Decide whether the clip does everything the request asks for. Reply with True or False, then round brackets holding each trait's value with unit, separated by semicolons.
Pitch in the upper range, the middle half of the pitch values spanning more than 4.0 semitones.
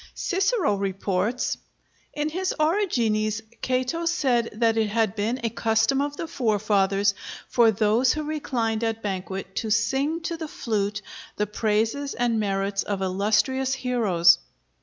True (225 Hz; 4.6 semitones)